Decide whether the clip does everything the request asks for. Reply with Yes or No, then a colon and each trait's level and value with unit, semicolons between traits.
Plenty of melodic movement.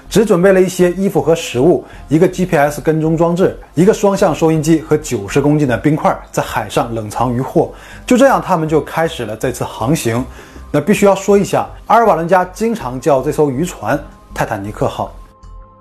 Yes: wide, 6.1 semitones